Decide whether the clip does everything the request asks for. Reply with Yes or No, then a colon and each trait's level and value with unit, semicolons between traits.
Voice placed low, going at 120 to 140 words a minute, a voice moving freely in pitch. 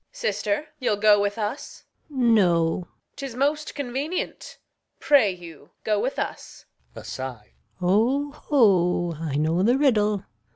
No: high, 215 Hz; slow, 135 wpm; wide, 7.6 semitones